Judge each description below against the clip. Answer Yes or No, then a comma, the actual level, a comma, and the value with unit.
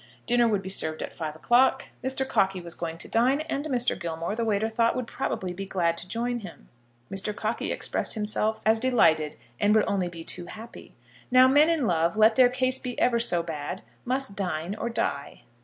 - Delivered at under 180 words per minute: No, fast, 205 wpm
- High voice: Yes, high, 215 Hz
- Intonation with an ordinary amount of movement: No, wide, 5.8 semitones